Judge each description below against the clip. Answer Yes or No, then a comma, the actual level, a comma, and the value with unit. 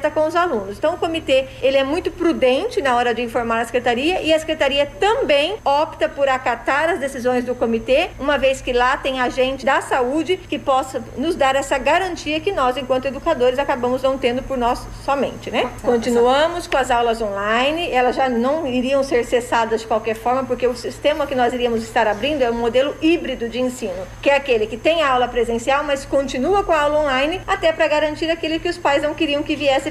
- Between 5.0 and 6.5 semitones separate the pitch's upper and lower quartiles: No, average, 3.5 semitones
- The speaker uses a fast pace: Yes, fast, 210 wpm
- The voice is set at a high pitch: Yes, very high, 270 Hz